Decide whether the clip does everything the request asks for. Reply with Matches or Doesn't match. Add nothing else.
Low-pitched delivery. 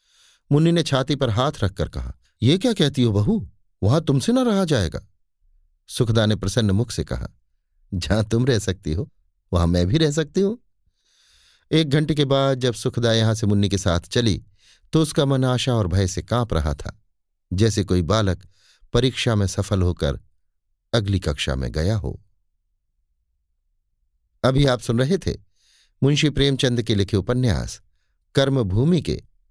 Matches